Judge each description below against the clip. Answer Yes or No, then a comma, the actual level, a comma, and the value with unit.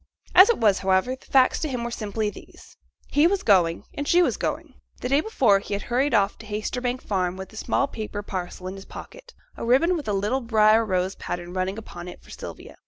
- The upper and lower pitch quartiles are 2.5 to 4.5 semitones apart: No, wide, 5.5 semitones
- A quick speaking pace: Yes, fast, 230 wpm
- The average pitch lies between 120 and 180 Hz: No, high, 220 Hz